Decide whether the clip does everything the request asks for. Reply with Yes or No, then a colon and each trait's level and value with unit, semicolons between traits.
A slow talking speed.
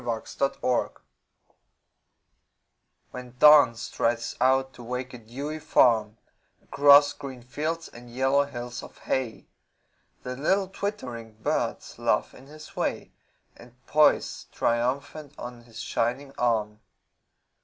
Yes: slow, 115 wpm